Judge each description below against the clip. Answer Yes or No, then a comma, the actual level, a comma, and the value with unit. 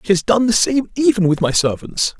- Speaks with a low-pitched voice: No, high, 205 Hz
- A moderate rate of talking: No, fast, 245 wpm